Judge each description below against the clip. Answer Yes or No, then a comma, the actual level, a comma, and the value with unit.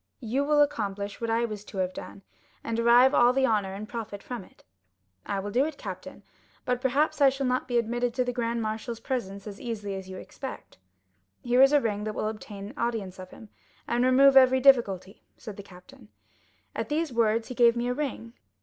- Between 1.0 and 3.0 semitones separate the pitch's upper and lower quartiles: No, average, 3.8 semitones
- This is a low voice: No, high, 235 Hz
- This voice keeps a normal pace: No, fast, 210 wpm